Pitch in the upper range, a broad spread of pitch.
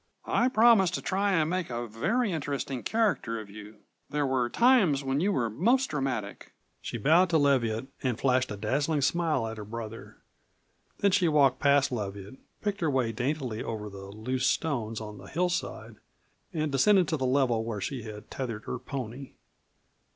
No: low, 135 Hz; wide, 6.4 semitones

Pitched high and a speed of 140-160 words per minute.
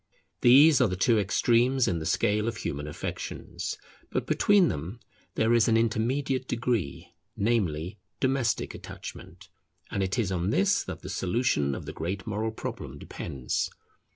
No: low, 110 Hz; average, 155 wpm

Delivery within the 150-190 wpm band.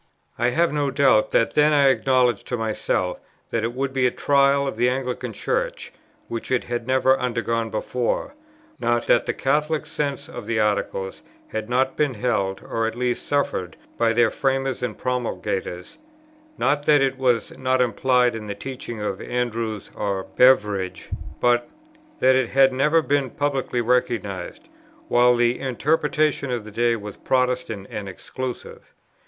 Yes: average, 160 wpm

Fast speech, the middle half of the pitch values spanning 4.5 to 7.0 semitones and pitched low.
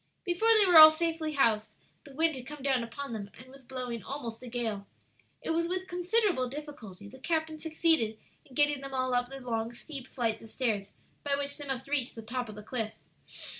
No: fast, 210 wpm; average, 5.0 semitones; very high, 265 Hz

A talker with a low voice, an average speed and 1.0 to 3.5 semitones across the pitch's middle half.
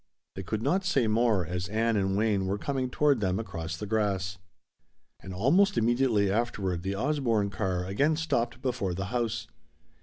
No: low, 110 Hz; average, 170 wpm; average, 4.5 semitones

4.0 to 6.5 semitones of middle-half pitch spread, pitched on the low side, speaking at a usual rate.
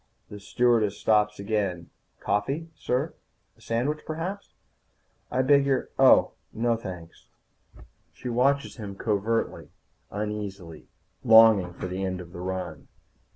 No: average, 4.4 semitones; low, 105 Hz; slow, 125 wpm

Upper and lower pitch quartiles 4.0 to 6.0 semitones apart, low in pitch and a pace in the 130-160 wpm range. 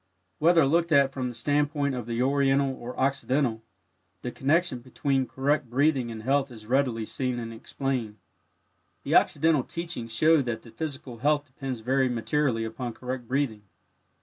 No: average, 3.0 semitones; low, 130 Hz; average, 155 wpm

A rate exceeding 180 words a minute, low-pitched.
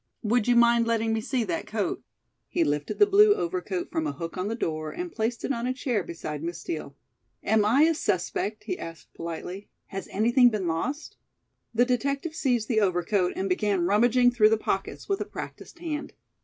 No: average, 195 wpm; high, 230 Hz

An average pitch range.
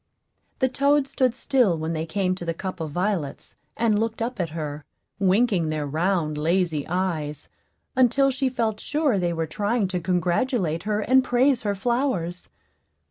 No: wide, 6.6 semitones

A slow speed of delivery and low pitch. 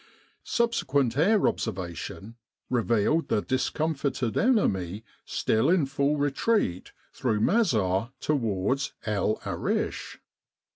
Yes: slow, 90 wpm; low, 130 Hz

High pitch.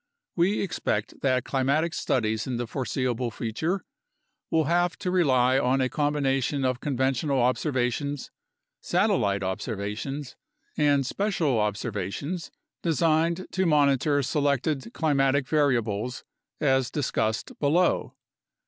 No: low, 135 Hz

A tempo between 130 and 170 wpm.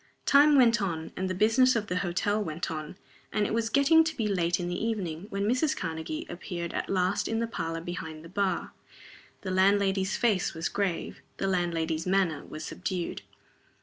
No: average, 185 wpm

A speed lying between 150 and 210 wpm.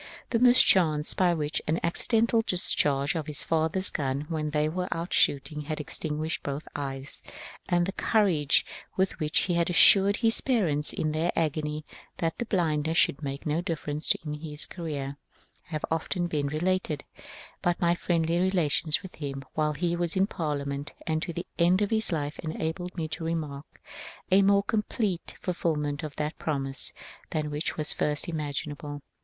Yes: average, 170 wpm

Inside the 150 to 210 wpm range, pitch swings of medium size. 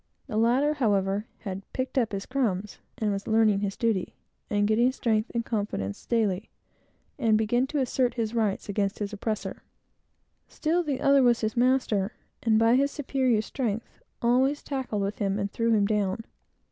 Yes: average, 165 wpm; average, 3.5 semitones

